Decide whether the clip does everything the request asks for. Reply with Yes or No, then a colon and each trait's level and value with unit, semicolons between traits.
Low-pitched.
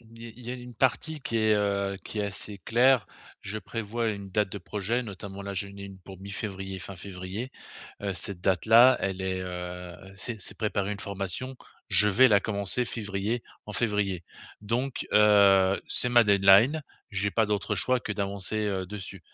Yes: low, 100 Hz